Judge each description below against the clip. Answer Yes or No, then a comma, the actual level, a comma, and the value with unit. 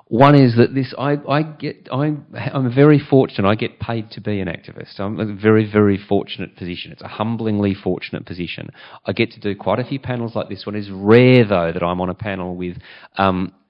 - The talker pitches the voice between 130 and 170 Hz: No, low, 105 Hz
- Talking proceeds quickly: Yes, fast, 220 wpm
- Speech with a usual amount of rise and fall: Yes, average, 4.6 semitones